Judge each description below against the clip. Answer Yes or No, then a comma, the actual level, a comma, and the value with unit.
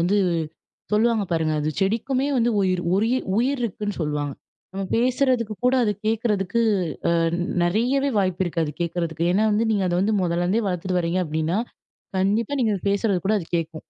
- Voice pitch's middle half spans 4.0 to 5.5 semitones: Yes, average, 4.7 semitones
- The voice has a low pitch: No, high, 195 Hz